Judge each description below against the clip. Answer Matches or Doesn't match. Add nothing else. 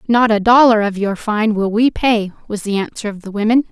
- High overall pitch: Matches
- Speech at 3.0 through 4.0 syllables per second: Doesn't match